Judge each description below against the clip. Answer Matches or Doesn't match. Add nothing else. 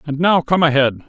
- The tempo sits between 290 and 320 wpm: Doesn't match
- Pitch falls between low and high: Matches